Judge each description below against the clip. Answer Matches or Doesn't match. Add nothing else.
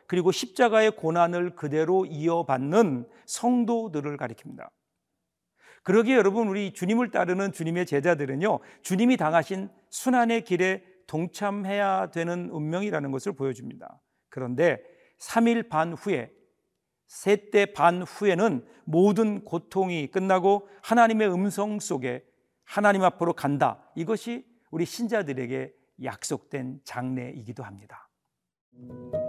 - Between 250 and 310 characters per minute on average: Matches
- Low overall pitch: Doesn't match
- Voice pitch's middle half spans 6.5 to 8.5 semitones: Doesn't match